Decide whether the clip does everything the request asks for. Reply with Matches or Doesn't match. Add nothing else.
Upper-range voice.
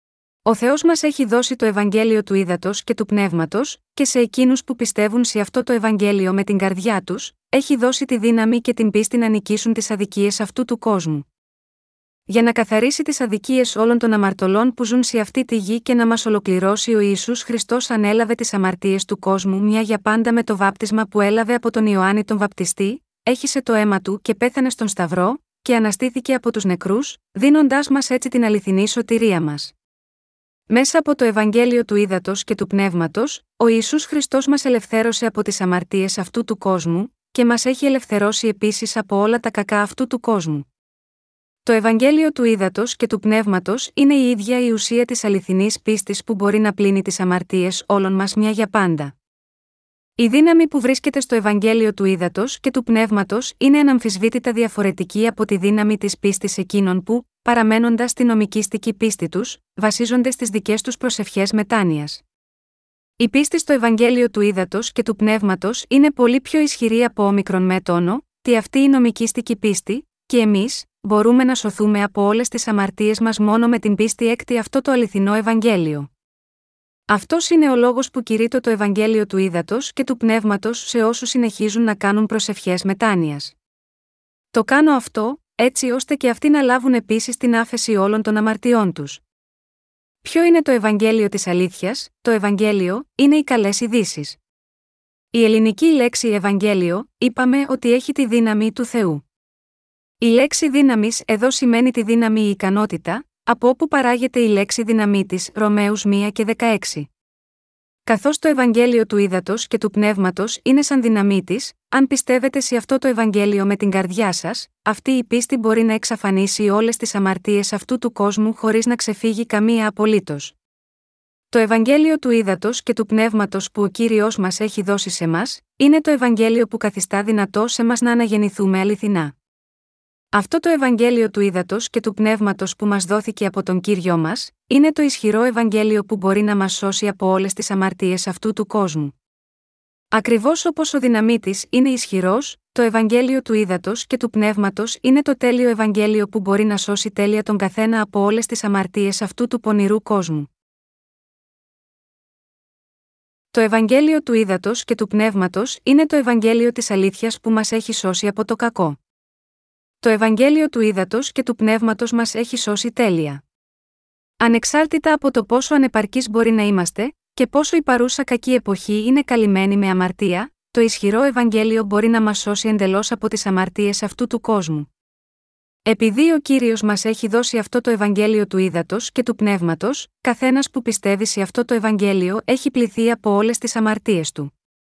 Matches